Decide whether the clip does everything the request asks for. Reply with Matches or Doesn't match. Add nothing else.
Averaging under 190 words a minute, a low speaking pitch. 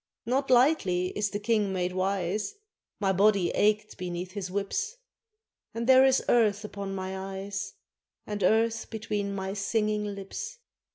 Doesn't match